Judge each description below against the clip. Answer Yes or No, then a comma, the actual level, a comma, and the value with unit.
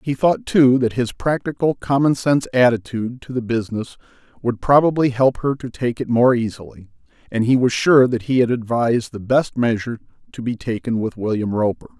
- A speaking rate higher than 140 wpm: Yes, average, 190 wpm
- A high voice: No, low, 120 Hz